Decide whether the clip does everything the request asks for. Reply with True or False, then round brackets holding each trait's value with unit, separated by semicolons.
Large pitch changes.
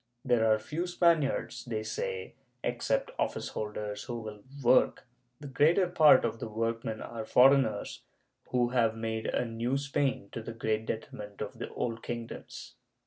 False (3.9 semitones)